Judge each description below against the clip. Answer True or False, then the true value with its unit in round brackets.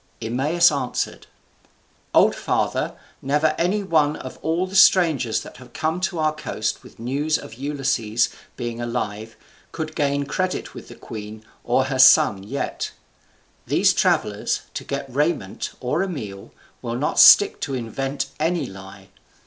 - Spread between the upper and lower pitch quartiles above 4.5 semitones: True (5.1 semitones)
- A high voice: False (140 Hz)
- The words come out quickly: False (150 wpm)